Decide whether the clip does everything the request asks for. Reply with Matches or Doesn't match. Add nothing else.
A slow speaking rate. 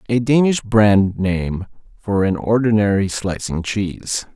Matches